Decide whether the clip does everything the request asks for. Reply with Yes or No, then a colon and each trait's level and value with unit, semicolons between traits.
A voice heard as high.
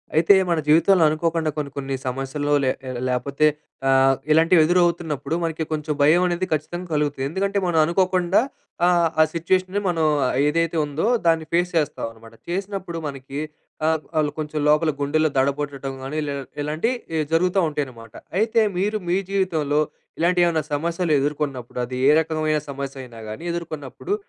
No: medium, 155 Hz